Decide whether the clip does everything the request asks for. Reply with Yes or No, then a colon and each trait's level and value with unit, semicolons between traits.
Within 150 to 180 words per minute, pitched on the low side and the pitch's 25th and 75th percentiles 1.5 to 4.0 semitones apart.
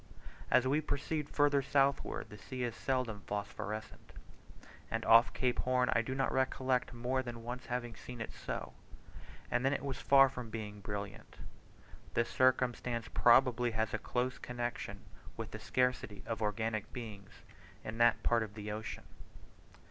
Yes: average, 155 wpm; low, 120 Hz; average, 2.8 semitones